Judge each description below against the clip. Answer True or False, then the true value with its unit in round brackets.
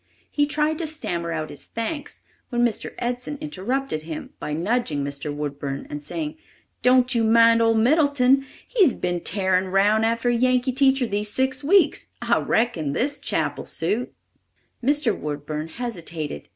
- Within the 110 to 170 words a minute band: True (150 wpm)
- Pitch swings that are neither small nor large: False (8.0 semitones)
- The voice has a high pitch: True (230 Hz)